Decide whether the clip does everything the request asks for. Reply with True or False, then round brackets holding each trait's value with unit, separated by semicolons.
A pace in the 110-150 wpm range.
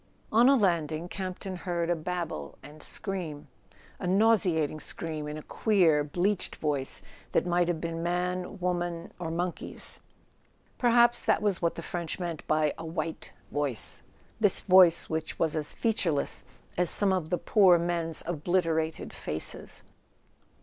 True (145 wpm)